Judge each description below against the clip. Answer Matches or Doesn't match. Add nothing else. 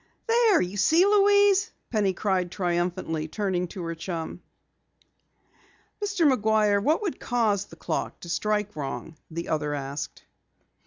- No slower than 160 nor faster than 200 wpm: Doesn't match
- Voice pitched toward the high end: Matches